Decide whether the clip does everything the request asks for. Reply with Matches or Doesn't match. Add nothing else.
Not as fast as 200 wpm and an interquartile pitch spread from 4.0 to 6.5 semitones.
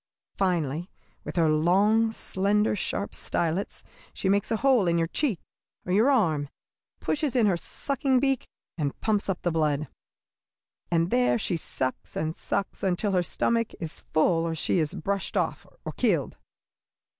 Matches